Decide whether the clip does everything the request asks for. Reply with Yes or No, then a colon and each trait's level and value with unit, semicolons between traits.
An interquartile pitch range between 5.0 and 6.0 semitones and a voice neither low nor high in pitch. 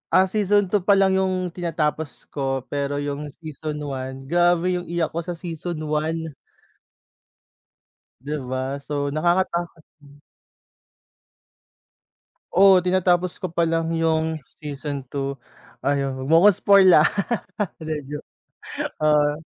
No: average, 3.6 semitones; medium, 160 Hz